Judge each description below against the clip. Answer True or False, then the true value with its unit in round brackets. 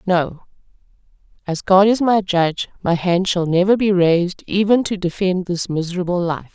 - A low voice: False (185 Hz)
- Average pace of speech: True (165 wpm)